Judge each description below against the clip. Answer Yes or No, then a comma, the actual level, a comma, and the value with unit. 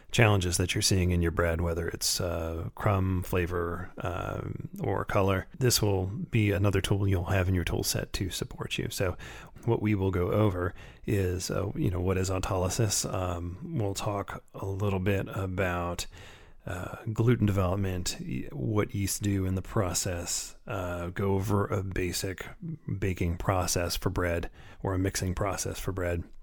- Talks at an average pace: Yes, average, 165 wpm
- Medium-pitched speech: No, very low, 95 Hz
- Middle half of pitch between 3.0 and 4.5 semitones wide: No, narrow, 2.5 semitones